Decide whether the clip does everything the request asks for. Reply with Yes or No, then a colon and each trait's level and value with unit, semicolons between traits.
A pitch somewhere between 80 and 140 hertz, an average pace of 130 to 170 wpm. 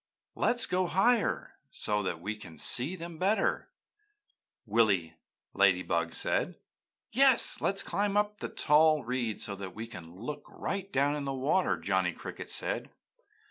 Yes: low, 135 Hz; average, 155 wpm